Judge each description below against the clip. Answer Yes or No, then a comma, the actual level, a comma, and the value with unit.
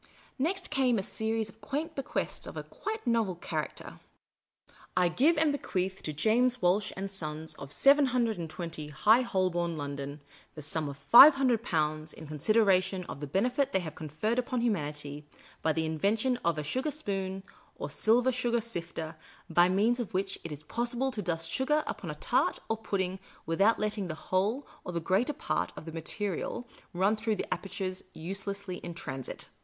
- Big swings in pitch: Yes, wide, 6.4 semitones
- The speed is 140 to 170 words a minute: No, average, 180 wpm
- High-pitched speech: Yes, high, 195 Hz